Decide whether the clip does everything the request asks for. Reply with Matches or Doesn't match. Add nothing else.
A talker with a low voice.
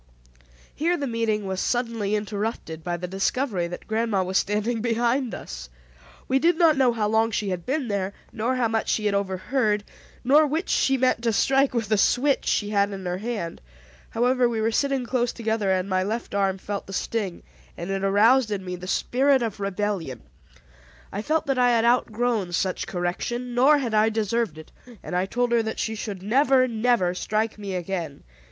Doesn't match